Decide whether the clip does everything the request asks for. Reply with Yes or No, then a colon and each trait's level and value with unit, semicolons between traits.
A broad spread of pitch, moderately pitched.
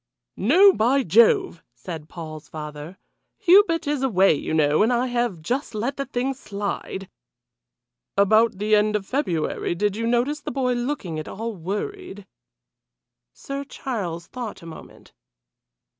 No: wide, 7.4 semitones; high, 215 Hz